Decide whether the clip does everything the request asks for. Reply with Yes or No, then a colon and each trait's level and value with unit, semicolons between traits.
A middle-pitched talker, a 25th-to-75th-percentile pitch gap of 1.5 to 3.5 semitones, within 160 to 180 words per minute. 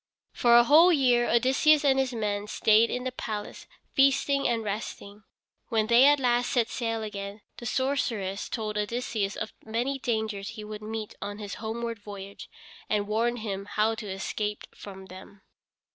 No: high, 220 Hz; average, 3.0 semitones; average, 165 wpm